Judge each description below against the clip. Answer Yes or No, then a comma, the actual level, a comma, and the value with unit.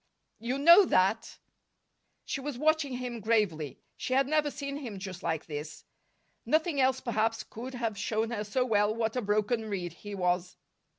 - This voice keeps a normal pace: Yes, average, 170 wpm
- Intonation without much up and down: No, average, 4.5 semitones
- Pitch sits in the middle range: No, high, 225 Hz